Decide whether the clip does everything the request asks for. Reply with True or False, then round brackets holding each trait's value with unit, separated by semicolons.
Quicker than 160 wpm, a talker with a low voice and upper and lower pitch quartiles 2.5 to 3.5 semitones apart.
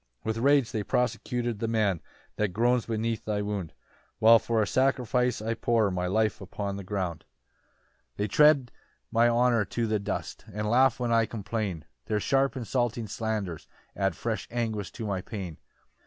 True (170 wpm; 110 Hz; 2.8 semitones)